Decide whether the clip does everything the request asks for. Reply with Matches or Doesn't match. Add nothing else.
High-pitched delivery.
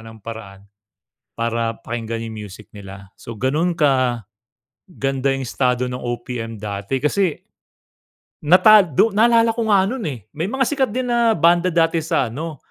Doesn't match